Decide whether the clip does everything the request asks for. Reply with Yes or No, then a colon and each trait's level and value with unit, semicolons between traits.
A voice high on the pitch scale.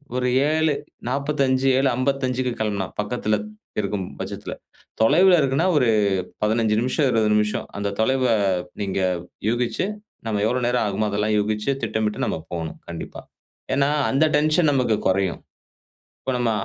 No: low, 120 Hz